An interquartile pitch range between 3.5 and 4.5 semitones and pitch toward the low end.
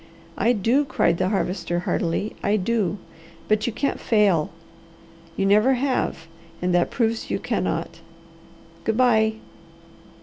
No: average, 4.2 semitones; high, 210 Hz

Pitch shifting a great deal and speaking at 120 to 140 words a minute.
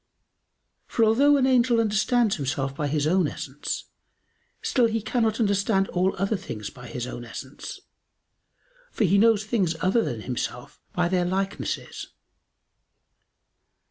Yes: wide, 7.6 semitones; slow, 135 wpm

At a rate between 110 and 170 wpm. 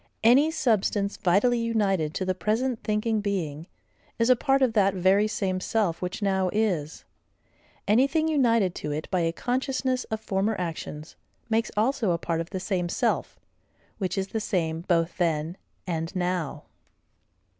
Yes: average, 155 wpm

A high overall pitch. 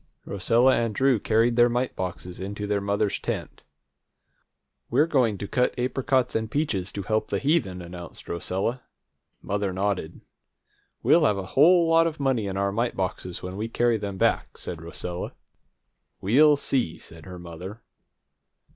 No: low, 105 Hz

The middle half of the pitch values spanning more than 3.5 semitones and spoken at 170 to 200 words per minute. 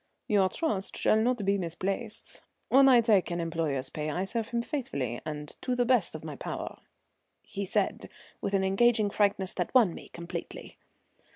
Yes: wide, 5.6 semitones; average, 175 wpm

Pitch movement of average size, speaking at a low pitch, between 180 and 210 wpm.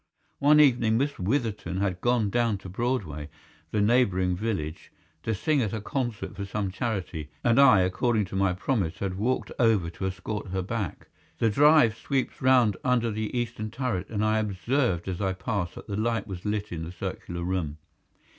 Yes: average, 4.2 semitones; low, 105 Hz; average, 185 wpm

